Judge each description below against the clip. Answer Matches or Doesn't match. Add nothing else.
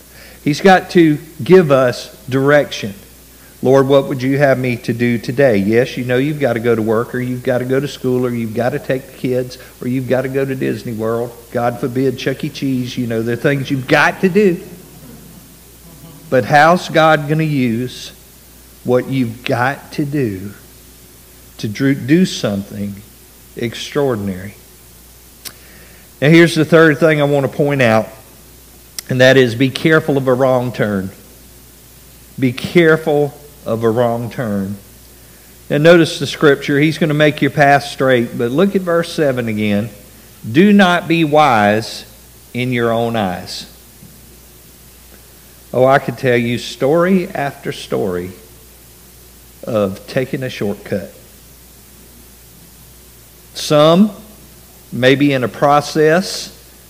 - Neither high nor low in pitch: Doesn't match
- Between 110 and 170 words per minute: Matches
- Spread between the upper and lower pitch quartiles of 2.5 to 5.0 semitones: Doesn't match